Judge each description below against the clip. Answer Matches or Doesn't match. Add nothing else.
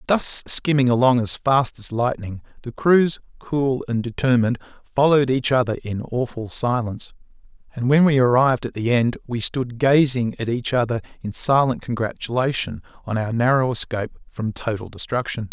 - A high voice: Doesn't match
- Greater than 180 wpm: Doesn't match